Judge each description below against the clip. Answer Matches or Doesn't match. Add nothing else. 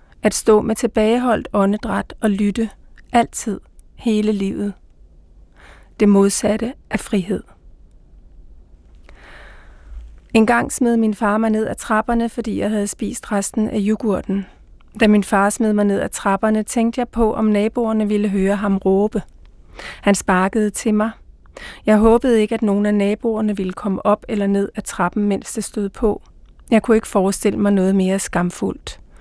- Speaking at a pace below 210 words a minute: Matches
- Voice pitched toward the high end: Matches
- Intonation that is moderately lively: Doesn't match